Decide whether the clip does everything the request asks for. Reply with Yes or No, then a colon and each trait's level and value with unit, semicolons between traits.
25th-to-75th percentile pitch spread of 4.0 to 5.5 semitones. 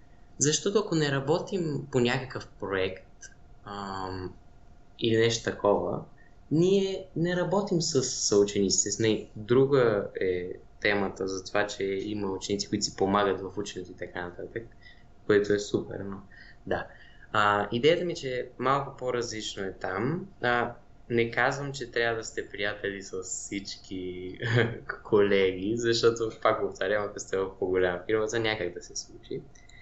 Yes: average, 4.6 semitones